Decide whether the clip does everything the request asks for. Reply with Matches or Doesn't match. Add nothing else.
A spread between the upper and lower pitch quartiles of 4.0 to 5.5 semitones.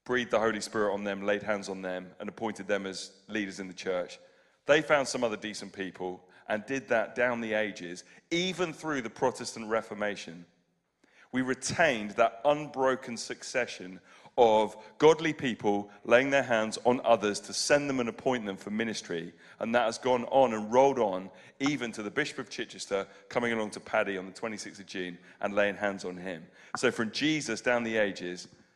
Matches